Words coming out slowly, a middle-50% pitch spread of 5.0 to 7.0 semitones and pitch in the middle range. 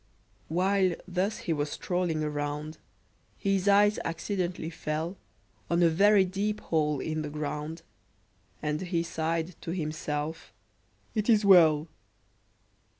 No: slow, 120 wpm; average, 3.6 semitones; medium, 165 Hz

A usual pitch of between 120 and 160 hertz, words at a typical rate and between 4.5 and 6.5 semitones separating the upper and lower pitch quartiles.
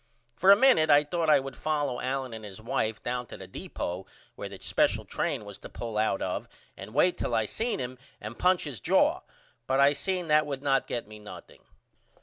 No: low, 135 Hz; fast, 215 wpm; wide, 5.6 semitones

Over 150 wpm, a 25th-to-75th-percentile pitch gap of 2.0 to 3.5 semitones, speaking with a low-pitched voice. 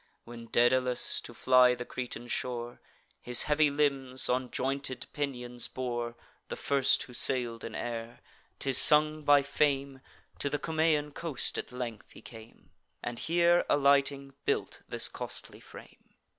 No: average, 145 wpm; average, 2.8 semitones; low, 130 Hz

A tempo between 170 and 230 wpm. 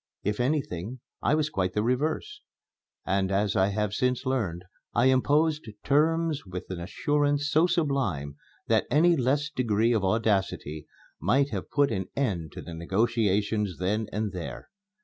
No: average, 150 wpm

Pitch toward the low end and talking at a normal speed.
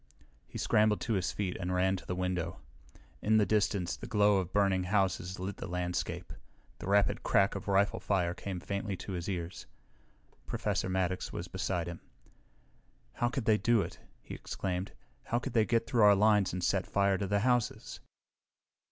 Yes: very low, 95 Hz; average, 180 wpm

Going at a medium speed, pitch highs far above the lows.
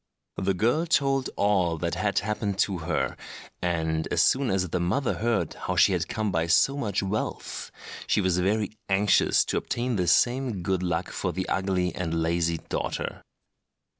No: average, 170 wpm; average, 3.7 semitones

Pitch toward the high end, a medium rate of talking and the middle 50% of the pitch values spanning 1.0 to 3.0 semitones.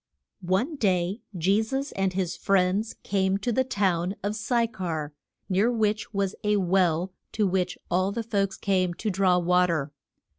Yes: high, 195 Hz; average, 170 wpm; average, 2.7 semitones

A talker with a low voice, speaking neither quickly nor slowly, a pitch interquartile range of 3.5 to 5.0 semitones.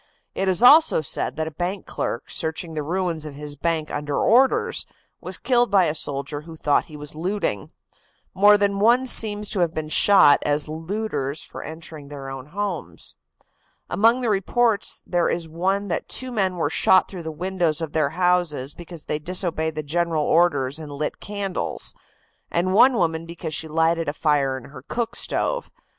No: medium, 165 Hz; average, 180 wpm; average, 4.4 semitones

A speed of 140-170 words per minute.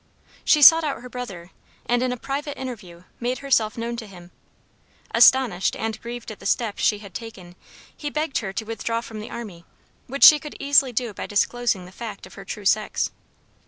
No: average, 195 wpm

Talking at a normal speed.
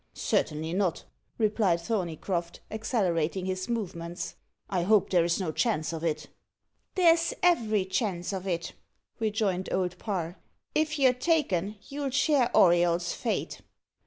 No: slow, 125 wpm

